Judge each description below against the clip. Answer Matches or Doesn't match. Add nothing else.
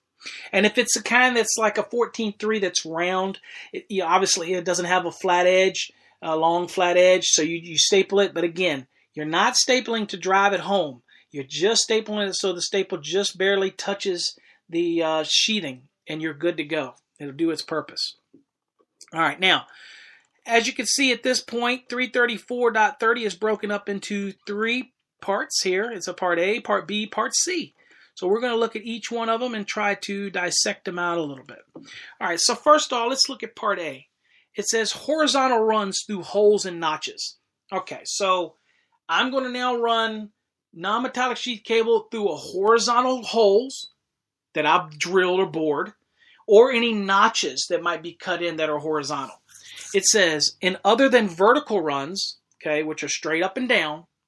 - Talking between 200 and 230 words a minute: Doesn't match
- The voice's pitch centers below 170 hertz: Doesn't match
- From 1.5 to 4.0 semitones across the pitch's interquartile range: Doesn't match